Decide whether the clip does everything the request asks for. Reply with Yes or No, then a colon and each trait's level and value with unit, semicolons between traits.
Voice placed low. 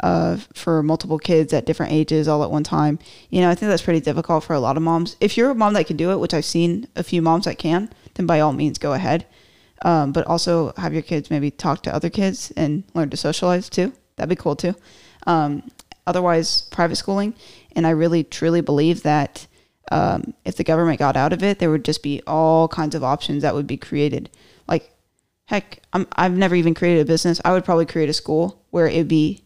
No: medium, 165 Hz